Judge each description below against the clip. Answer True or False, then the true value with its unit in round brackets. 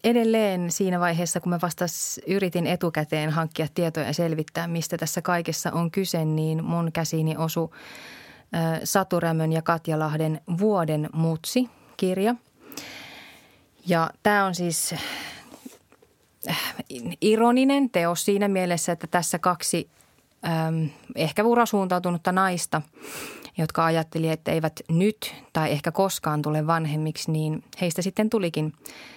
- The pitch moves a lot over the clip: False (2.7 semitones)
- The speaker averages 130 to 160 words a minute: False (115 wpm)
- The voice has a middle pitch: True (170 Hz)